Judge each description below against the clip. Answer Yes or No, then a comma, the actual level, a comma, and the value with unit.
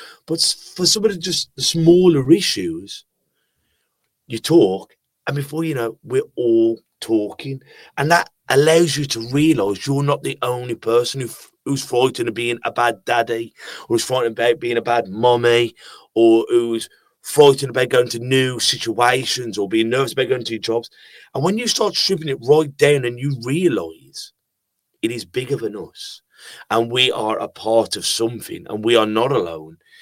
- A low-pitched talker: Yes, low, 125 Hz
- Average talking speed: Yes, average, 175 wpm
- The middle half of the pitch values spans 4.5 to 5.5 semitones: Yes, average, 5.2 semitones